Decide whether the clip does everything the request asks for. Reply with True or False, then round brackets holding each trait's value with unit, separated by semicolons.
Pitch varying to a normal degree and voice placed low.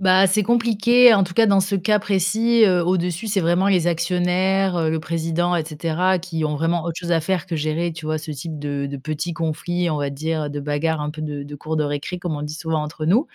False (3.3 semitones; 170 Hz)